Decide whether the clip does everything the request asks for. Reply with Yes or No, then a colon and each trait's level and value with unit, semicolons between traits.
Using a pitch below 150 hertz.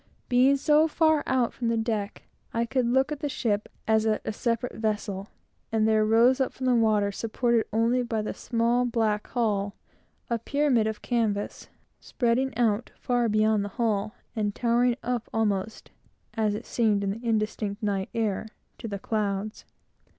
No: high, 225 Hz